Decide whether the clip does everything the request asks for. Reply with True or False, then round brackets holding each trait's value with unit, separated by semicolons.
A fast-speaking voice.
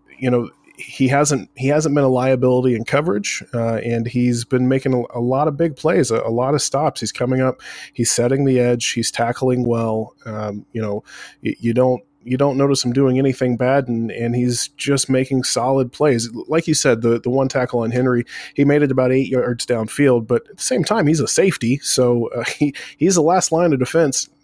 True (220 wpm)